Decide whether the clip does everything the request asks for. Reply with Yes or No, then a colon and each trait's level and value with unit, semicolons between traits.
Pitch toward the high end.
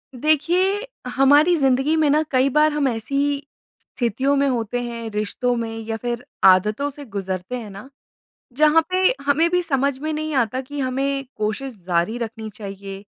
Yes: very high, 265 Hz